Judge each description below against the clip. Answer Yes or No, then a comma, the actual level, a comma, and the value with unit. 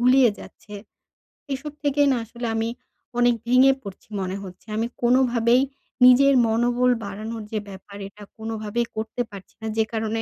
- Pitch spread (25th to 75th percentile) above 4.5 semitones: No, narrow, 2.6 semitones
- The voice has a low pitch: No, high, 230 Hz